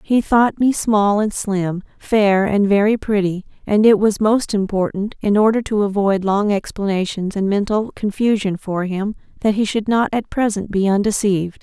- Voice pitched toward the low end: No, high, 205 Hz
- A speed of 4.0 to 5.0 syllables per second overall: Yes, 4.6 syllables/s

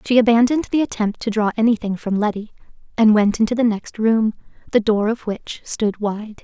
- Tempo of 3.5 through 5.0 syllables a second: No, 5.4 syllables/s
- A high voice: Yes, high, 220 Hz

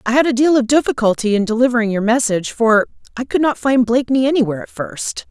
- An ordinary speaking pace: No, fast, 215 wpm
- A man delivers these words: No, female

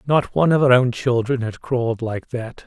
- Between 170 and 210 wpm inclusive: No, fast, 225 wpm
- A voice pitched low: Yes, low, 125 Hz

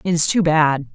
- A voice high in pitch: No, medium, 160 Hz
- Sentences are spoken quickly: Yes, fast, 255 wpm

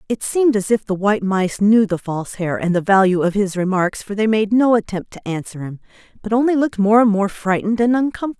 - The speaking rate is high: Yes, fast, 245 wpm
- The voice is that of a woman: Yes, female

